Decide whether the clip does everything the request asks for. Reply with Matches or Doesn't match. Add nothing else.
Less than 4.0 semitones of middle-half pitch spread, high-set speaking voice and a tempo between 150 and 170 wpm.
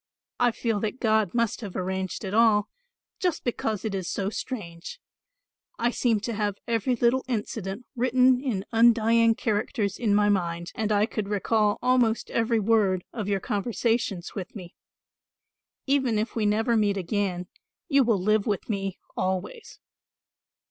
Matches